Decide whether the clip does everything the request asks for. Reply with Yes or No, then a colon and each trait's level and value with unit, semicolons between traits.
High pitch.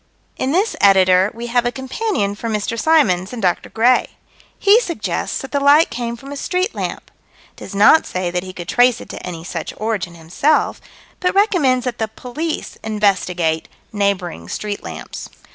Yes: high, 225 Hz